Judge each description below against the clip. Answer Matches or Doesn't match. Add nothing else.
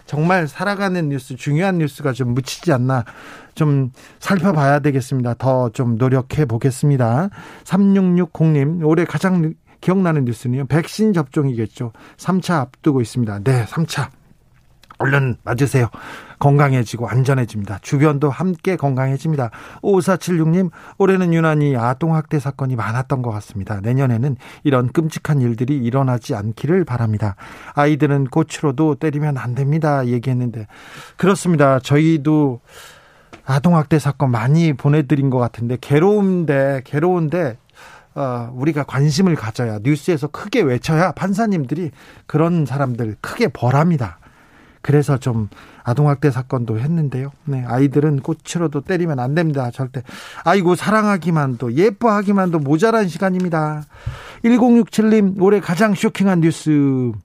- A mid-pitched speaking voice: Matches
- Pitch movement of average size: Matches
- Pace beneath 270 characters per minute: Doesn't match